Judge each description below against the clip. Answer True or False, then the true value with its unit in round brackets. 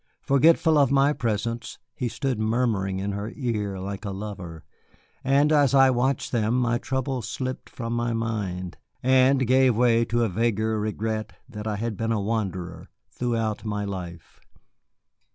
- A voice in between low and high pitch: False (115 Hz)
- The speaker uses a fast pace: False (155 wpm)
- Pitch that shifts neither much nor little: True (3.7 semitones)